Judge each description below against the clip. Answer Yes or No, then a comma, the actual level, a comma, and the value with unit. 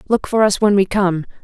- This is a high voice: Yes, high, 200 Hz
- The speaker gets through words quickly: Yes, fast, 250 wpm